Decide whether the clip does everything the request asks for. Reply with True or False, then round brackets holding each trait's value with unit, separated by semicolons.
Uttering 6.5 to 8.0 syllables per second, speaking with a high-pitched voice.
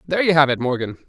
False (7.8 syllables/s; 145 Hz)